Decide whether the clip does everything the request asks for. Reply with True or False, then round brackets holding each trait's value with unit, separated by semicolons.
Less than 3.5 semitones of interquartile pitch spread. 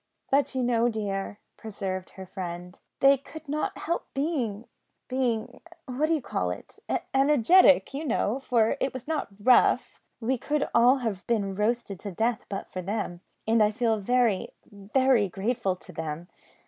False (5.1 semitones)